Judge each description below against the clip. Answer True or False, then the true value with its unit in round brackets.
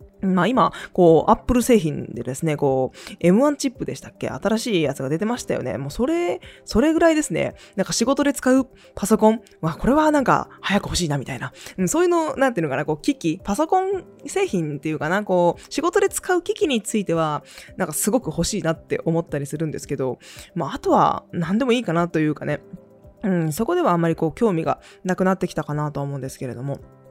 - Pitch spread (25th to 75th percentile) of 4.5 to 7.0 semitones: False (7.6 semitones)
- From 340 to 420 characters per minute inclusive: True (385 characters per minute)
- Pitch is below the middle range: False (185 Hz)